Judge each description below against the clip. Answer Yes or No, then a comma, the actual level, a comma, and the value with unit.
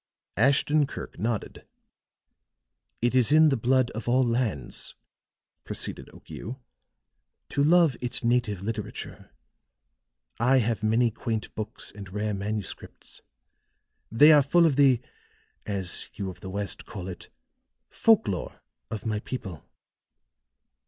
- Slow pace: Yes, slow, 125 wpm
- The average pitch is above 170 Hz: No, low, 115 Hz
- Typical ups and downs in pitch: Yes, average, 4.1 semitones